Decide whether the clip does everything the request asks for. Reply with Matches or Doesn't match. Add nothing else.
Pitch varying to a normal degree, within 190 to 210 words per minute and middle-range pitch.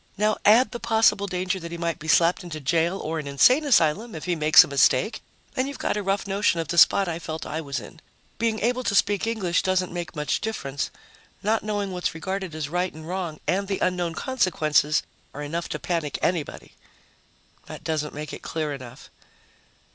Matches